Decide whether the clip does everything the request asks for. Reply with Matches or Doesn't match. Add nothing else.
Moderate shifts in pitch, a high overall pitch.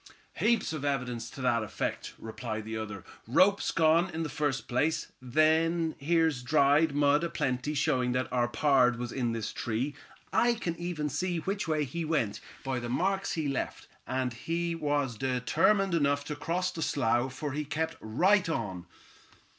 Doesn't match